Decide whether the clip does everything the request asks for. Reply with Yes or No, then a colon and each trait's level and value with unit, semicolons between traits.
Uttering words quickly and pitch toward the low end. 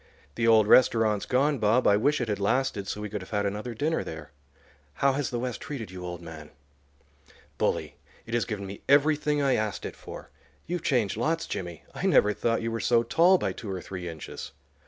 Yes: fast, 210 wpm; low, 115 Hz